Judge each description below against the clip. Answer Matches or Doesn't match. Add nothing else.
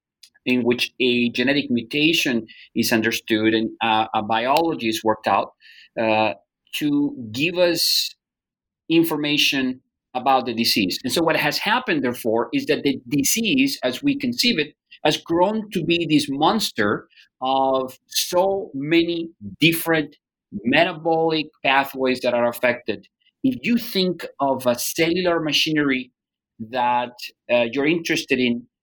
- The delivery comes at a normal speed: Doesn't match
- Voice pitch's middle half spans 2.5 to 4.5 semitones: Doesn't match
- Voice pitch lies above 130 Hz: Matches